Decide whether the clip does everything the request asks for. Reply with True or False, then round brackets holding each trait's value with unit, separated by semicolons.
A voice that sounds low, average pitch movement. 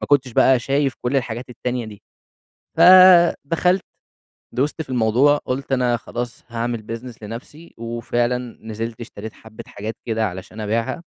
True (120 Hz; 3.3 semitones)